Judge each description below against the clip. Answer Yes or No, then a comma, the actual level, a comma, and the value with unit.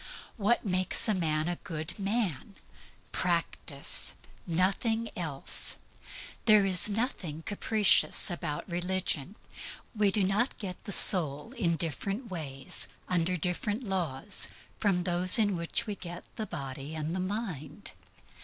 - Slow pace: Yes, slow, 125 wpm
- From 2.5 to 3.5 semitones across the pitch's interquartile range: No, average, 4.0 semitones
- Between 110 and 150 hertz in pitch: No, medium, 185 Hz